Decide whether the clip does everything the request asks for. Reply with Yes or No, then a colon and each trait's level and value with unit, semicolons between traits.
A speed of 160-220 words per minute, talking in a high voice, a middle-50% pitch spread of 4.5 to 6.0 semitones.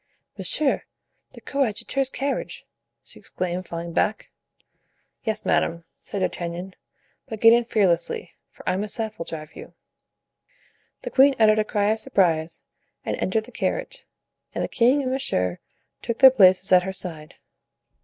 No: average, 145 wpm; high, 205 Hz; average, 5.2 semitones